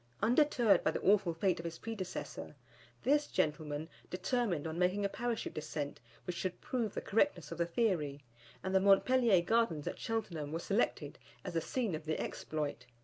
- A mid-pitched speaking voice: Yes, medium, 180 Hz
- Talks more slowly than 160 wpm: No, average, 175 wpm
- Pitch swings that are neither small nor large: No, wide, 6.1 semitones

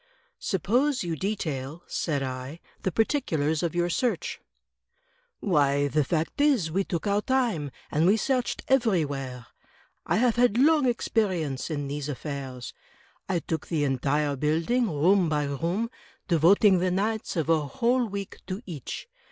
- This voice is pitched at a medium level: Yes, medium, 170 Hz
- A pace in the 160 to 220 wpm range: No, average, 150 wpm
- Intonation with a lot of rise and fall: Yes, wide, 6.8 semitones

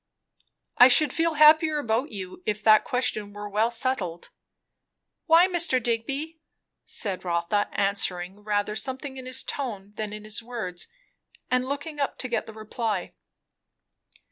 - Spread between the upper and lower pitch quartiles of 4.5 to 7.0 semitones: Yes, average, 4.9 semitones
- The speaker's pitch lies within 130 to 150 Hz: No, high, 230 Hz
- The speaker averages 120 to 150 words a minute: Yes, average, 145 wpm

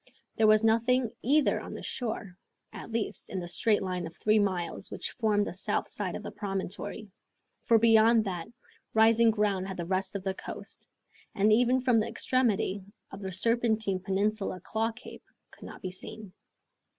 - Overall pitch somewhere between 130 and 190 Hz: No, high, 210 Hz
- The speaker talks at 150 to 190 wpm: Yes, average, 175 wpm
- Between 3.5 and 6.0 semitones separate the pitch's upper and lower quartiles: No, average, 3.0 semitones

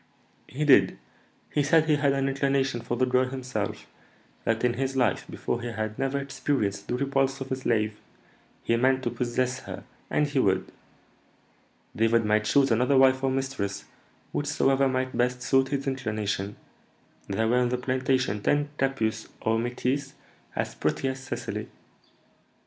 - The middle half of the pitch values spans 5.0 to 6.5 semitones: No, narrow, 2.6 semitones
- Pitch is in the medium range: No, low, 130 Hz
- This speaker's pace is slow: No, average, 160 wpm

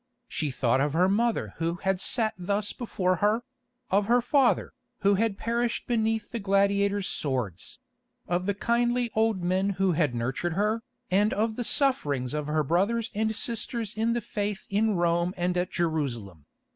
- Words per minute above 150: Yes, average, 170 wpm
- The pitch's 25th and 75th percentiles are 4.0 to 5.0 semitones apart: Yes, average, 4.6 semitones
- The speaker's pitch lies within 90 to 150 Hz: No, high, 200 Hz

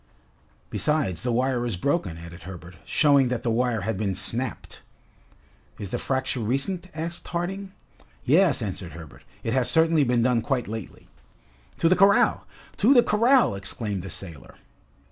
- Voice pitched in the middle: No, low, 125 Hz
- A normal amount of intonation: No, wide, 8.4 semitones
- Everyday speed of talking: Yes, average, 155 wpm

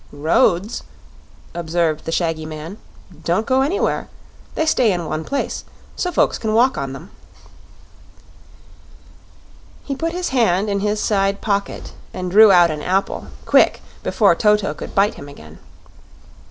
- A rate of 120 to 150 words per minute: Yes, average, 140 wpm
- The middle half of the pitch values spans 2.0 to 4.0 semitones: No, average, 4.7 semitones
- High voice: Yes, high, 195 Hz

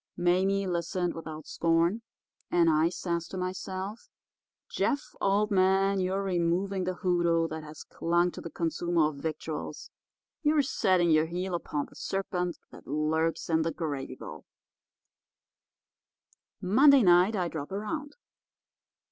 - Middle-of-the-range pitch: Yes, medium, 175 Hz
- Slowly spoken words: Yes, slow, 130 wpm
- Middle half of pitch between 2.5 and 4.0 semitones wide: Yes, average, 2.8 semitones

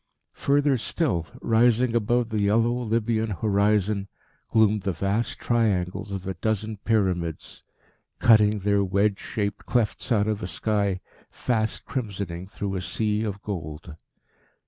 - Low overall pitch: Yes, low, 105 Hz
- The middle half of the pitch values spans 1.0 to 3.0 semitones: Yes, narrow, 2.4 semitones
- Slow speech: Yes, slow, 130 wpm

